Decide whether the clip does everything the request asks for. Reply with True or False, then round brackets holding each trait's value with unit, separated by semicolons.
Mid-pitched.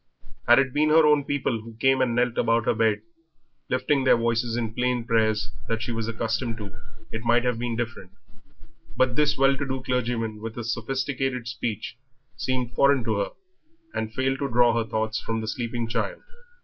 False (120 Hz)